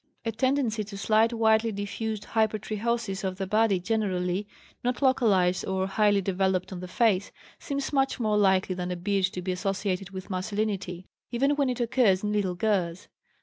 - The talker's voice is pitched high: Yes, high, 205 Hz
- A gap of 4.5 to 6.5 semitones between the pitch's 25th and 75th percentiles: No, average, 3.1 semitones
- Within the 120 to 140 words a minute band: No, average, 170 wpm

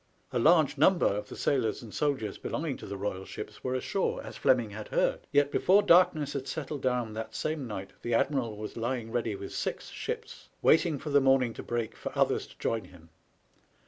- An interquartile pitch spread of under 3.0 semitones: No, average, 4.9 semitones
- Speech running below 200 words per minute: No, fast, 205 wpm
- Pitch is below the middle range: Yes, low, 125 Hz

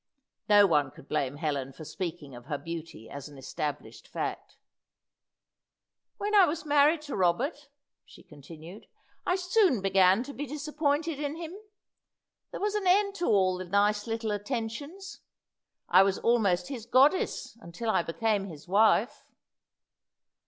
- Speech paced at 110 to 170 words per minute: Yes, average, 145 wpm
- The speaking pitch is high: Yes, high, 210 Hz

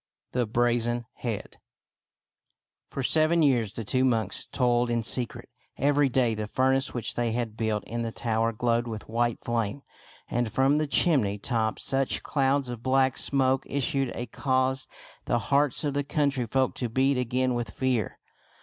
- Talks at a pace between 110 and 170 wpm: Yes, average, 165 wpm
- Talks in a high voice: No, low, 125 Hz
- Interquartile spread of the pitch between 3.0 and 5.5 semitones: No, narrow, 2.5 semitones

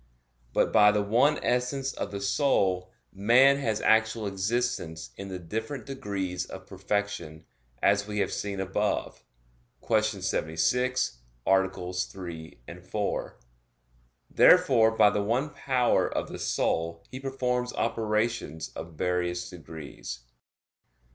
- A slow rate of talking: Yes, slow, 120 wpm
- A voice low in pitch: Yes, low, 100 Hz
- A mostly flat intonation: No, average, 4.6 semitones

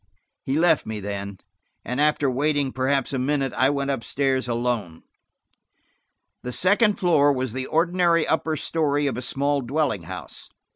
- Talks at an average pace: Yes, average, 155 wpm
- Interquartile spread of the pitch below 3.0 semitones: No, average, 3.4 semitones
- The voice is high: No, medium, 140 Hz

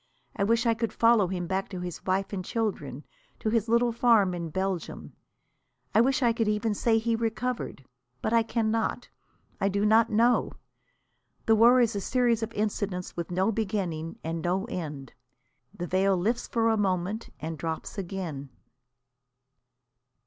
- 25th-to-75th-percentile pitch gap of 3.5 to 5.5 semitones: Yes, average, 4.0 semitones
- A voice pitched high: Yes, high, 210 Hz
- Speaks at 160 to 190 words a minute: Yes, average, 165 wpm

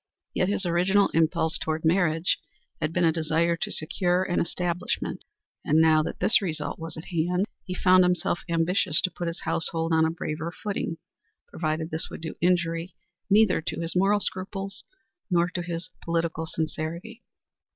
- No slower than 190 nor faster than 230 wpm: No, average, 165 wpm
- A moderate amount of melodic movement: No, narrow, 2.1 semitones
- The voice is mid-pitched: Yes, medium, 170 Hz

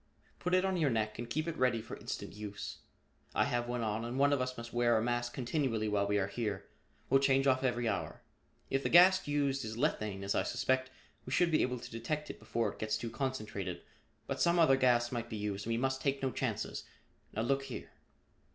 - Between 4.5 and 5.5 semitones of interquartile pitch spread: No, average, 3.7 semitones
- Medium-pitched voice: No, low, 120 Hz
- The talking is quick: Yes, fast, 230 wpm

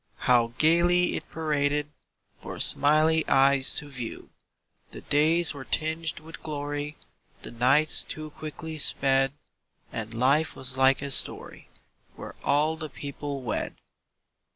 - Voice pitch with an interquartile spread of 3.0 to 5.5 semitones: No, narrow, 2.6 semitones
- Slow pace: Yes, slow, 130 wpm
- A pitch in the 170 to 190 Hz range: No, medium, 145 Hz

